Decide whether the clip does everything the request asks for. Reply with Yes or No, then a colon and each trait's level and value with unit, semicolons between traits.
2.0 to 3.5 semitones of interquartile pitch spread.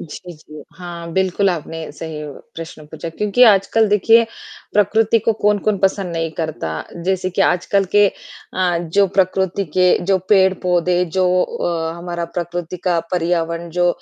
Yes: narrow, 2.6 semitones